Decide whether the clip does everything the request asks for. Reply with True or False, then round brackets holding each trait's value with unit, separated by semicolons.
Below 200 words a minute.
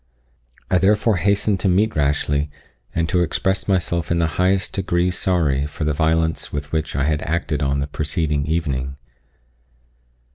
True (155 wpm)